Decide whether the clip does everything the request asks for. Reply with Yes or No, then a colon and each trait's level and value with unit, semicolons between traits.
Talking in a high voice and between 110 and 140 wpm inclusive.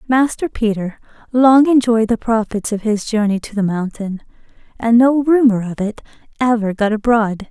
No: high, 225 Hz; average, 160 wpm